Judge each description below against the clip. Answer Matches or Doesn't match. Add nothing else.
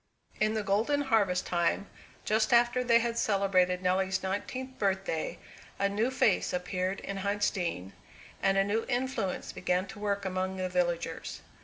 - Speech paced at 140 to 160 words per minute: Matches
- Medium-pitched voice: Doesn't match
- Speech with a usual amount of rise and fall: Matches